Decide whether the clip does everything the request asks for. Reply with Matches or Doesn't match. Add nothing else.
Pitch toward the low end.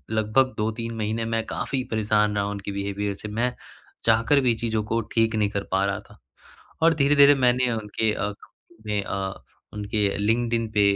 Matches